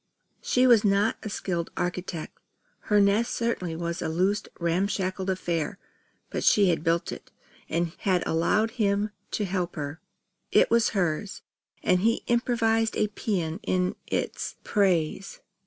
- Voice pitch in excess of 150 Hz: Yes, high, 190 Hz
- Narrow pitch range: No, average, 3.7 semitones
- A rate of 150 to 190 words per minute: No, average, 140 wpm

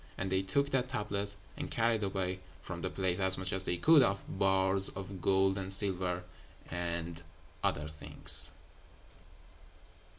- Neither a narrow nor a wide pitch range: No, narrow, 1.5 semitones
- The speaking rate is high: No, average, 145 wpm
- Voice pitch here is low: Yes, very low, 95 Hz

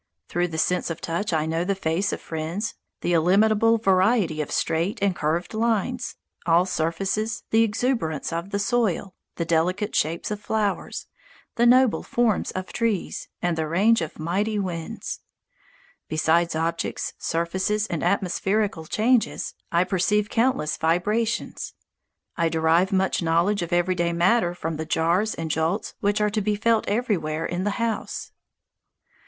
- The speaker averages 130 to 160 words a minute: Yes, average, 150 wpm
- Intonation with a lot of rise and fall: No, average, 4.3 semitones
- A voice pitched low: No, medium, 185 Hz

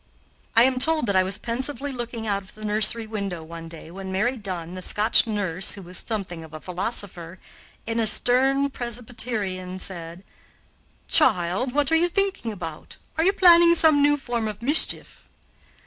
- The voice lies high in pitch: Yes, high, 220 Hz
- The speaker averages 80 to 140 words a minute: No, average, 175 wpm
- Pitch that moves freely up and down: Yes, wide, 5.9 semitones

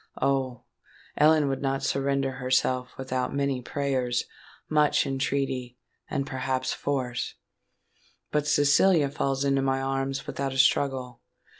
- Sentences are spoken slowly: Yes, slow, 105 wpm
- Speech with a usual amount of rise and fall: No, narrow, 1.2 semitones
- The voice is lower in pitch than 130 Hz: No, low, 135 Hz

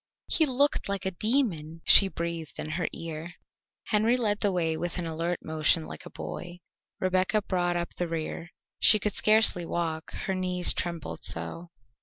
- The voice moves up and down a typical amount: Yes, average, 3.3 semitones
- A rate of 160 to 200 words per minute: Yes, average, 170 wpm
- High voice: No, medium, 175 Hz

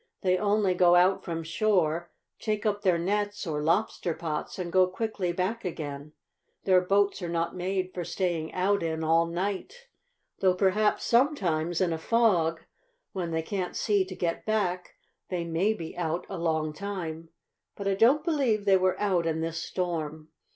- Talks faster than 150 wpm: Yes, average, 170 wpm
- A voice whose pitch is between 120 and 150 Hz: No, medium, 180 Hz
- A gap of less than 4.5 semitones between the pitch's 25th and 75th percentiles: Yes, average, 3.4 semitones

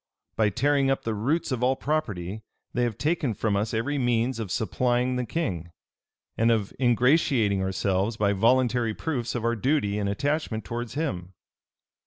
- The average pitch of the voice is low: Yes, low, 115 Hz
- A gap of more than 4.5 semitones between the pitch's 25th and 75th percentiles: No, average, 4.1 semitones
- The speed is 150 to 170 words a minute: Yes, average, 165 wpm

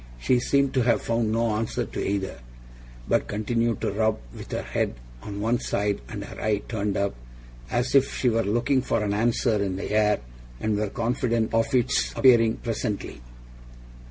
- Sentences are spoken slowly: No, average, 180 wpm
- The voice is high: No, low, 110 Hz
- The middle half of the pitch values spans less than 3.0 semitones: Yes, narrow, 2.5 semitones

